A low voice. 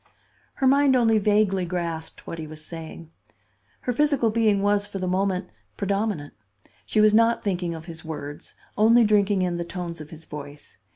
No: high, 190 Hz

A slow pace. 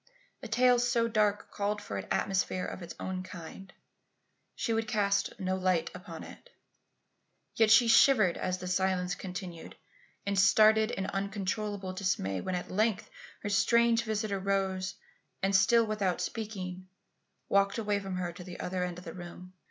No: average, 160 wpm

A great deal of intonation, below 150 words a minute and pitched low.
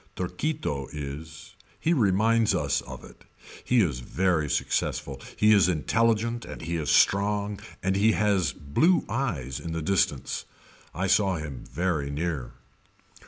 Yes: wide, 6.0 semitones; average, 140 wpm; very low, 90 Hz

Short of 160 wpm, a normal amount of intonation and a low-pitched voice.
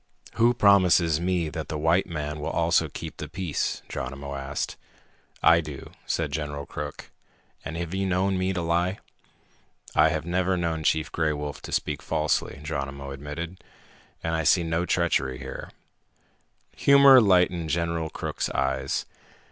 Yes: average, 150 wpm; average, 3.3 semitones; very low, 80 Hz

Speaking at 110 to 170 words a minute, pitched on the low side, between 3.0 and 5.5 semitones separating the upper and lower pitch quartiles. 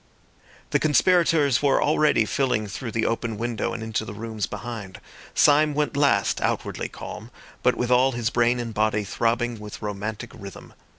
Yes: average, 165 wpm; low, 120 Hz; average, 3.7 semitones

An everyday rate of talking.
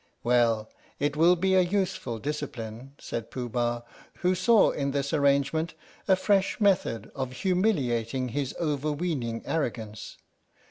No: slow, 130 wpm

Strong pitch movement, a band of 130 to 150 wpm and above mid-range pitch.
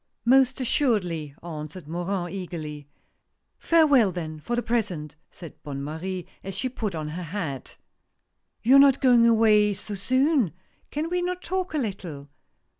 No: wide, 8.1 semitones; average, 165 wpm; high, 195 Hz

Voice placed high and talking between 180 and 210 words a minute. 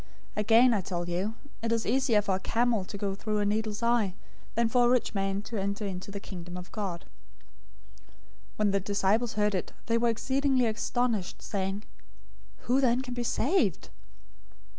Yes: high, 215 Hz; average, 185 wpm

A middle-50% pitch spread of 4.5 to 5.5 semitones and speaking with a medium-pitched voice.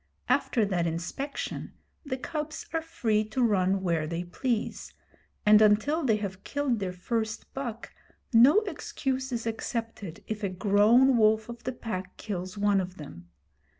No: average, 5.2 semitones; high, 220 Hz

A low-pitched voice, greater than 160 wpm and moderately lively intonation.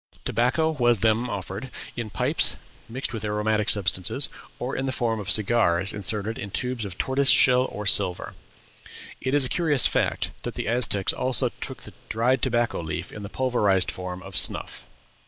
Yes: low, 110 Hz; average, 175 wpm; average, 4.1 semitones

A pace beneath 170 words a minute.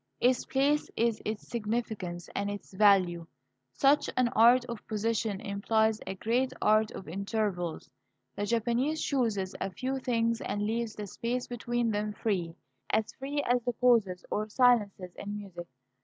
Yes: average, 155 wpm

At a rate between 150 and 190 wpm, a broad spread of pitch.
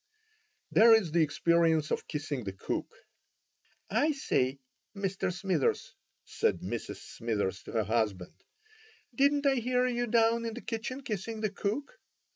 No: average, 140 wpm; wide, 8.4 semitones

